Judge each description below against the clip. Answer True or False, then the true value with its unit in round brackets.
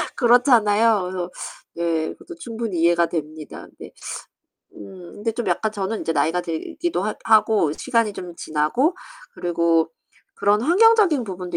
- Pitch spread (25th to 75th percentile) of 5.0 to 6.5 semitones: True (5.4 semitones)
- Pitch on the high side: True (200 Hz)